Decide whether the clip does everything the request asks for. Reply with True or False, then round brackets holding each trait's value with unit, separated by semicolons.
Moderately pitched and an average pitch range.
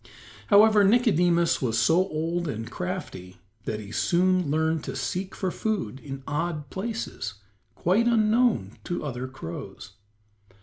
False (170 Hz; 6.4 semitones)